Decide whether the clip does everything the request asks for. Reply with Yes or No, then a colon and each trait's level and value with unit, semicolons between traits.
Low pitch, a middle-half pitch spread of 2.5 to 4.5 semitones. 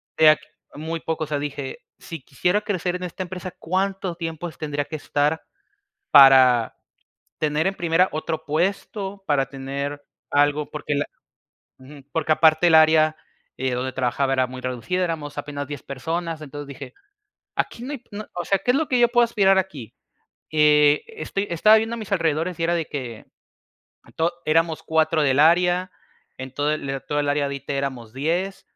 No: medium, 155 Hz; average, 3.9 semitones